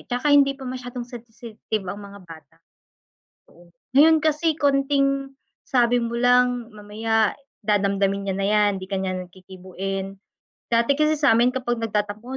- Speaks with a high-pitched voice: Yes, high, 230 Hz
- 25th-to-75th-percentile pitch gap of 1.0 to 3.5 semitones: No, average, 4.9 semitones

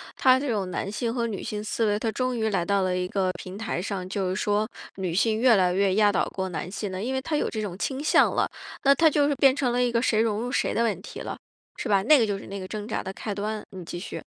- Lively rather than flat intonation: No, average, 3.9 semitones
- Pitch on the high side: Yes, high, 210 Hz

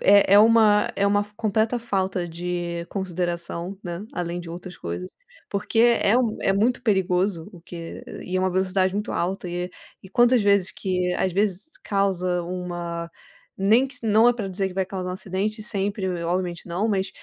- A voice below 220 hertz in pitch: Yes, high, 190 Hz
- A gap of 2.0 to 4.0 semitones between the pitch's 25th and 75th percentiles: Yes, average, 2.7 semitones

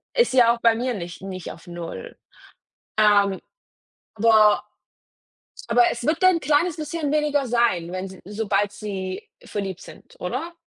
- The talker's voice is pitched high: Yes, high, 220 Hz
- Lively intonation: Yes, wide, 6.9 semitones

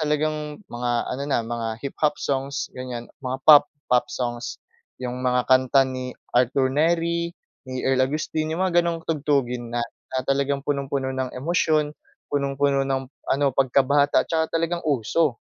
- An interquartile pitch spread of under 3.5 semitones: Yes, average, 2.9 semitones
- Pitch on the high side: No, low, 135 Hz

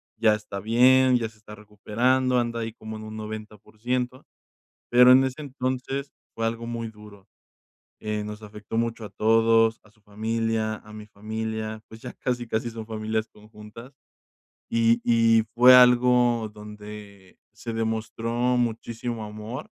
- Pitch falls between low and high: No, low, 110 Hz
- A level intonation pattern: Yes, narrow, 1.9 semitones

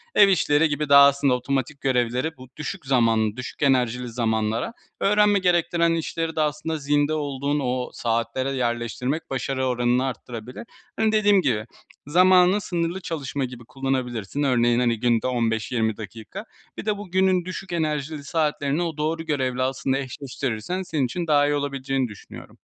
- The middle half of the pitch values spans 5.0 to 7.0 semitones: No, average, 4.6 semitones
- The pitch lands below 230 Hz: Yes, medium, 140 Hz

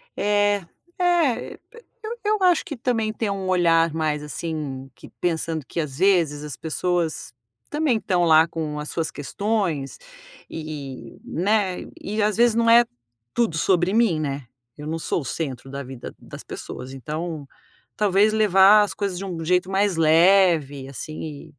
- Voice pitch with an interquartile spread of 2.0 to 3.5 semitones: No, average, 5.2 semitones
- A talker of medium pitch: Yes, medium, 175 Hz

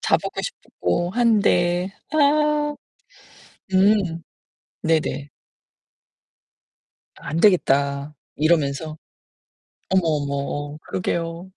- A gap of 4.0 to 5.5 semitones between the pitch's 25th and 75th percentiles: Yes, average, 5.2 semitones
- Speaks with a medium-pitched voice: Yes, medium, 170 Hz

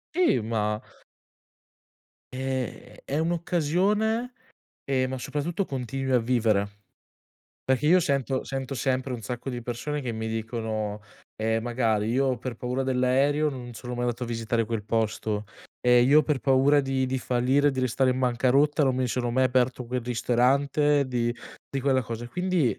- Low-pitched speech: Yes, low, 130 Hz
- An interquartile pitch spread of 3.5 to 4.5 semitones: No, average, 2.7 semitones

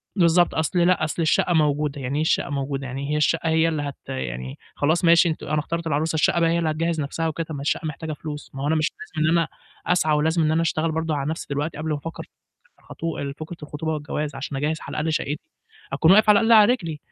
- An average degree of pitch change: No, narrow, 2.0 semitones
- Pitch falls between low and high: Yes, medium, 155 Hz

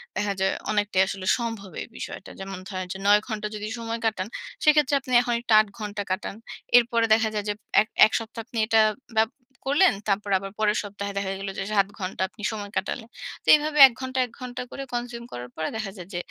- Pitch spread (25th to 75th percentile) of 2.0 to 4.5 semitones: Yes, average, 3.1 semitones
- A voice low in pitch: No, high, 210 Hz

